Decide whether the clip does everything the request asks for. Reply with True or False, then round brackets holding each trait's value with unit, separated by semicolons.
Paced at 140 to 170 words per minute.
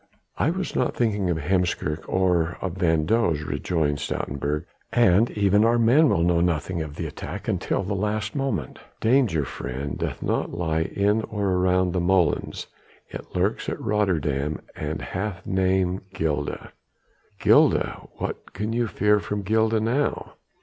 True (150 wpm)